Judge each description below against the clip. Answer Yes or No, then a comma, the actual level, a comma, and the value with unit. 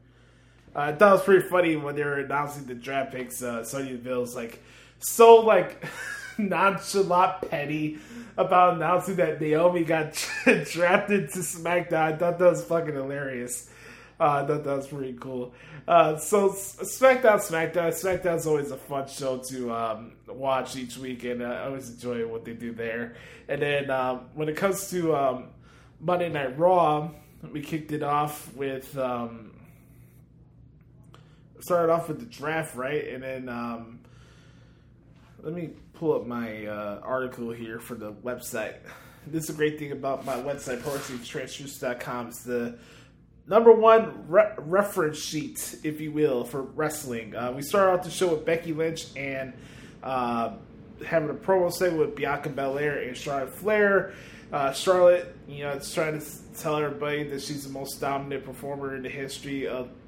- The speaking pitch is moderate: Yes, medium, 145 Hz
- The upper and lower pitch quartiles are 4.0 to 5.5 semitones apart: Yes, average, 4.6 semitones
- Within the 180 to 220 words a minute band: No, average, 165 wpm